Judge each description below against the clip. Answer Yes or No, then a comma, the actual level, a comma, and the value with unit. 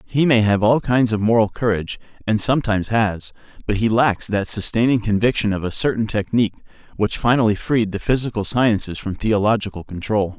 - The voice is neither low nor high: No, low, 110 Hz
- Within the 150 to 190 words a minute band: Yes, average, 175 wpm